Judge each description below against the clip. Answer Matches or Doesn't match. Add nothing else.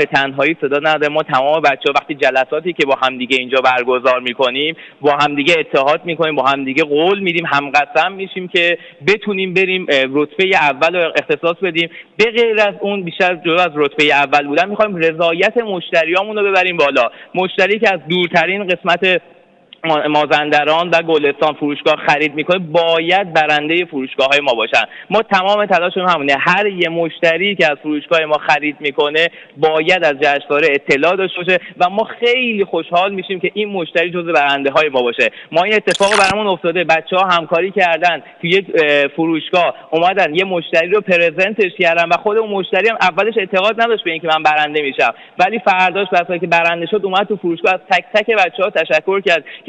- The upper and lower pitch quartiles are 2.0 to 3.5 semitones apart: Doesn't match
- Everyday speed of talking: Doesn't match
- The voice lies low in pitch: Doesn't match